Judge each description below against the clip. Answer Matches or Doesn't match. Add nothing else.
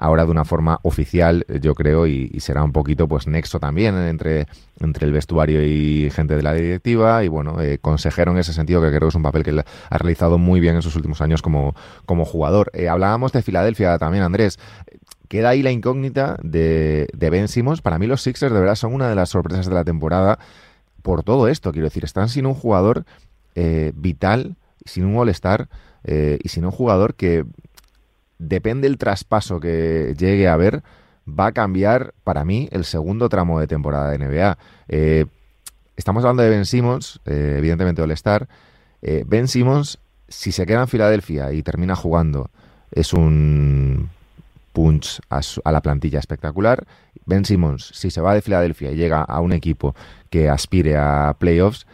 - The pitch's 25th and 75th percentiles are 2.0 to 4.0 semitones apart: Doesn't match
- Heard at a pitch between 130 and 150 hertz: Doesn't match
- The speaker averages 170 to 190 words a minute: Matches